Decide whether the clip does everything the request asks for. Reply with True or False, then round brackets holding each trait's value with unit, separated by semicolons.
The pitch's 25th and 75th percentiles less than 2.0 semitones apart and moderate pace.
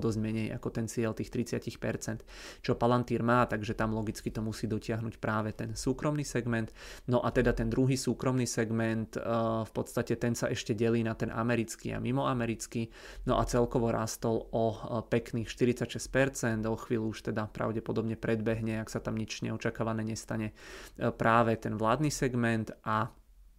True (1.3 semitones; 160 wpm)